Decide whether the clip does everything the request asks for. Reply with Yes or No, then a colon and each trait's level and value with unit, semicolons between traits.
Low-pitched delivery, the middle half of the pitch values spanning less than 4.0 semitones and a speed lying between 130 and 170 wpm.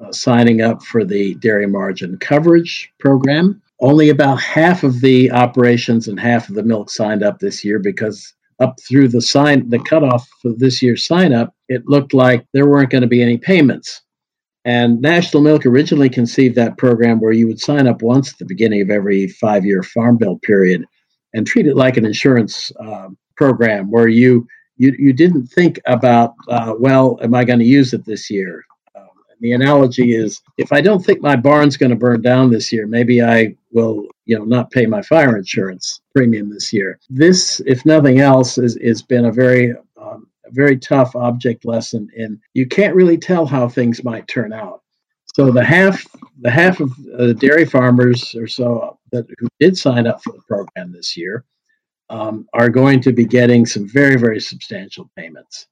No: low, 125 Hz; average, 3.0 semitones; average, 190 wpm